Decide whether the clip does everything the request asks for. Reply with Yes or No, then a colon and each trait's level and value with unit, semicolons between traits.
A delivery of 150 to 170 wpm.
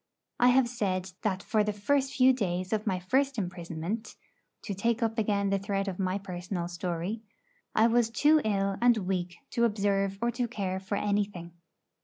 No: average, 180 wpm